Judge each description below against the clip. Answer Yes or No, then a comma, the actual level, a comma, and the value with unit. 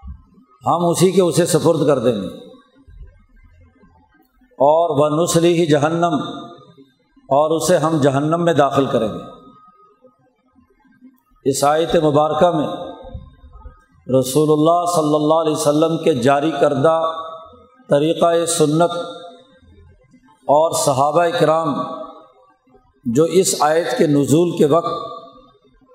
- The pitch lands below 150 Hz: No, medium, 160 Hz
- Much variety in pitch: No, average, 3.1 semitones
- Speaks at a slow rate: Yes, slow, 105 wpm